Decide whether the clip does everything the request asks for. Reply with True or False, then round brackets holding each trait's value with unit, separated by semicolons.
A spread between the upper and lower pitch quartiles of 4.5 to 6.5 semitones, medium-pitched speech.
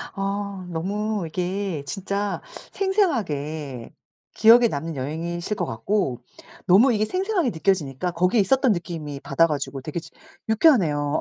True (5.6 semitones; 180 Hz)